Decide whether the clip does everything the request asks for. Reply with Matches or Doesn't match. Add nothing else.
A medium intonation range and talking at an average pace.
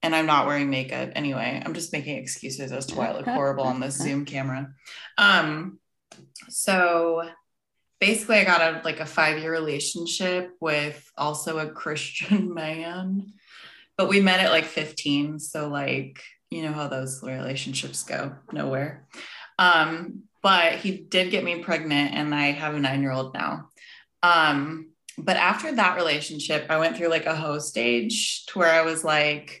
Matches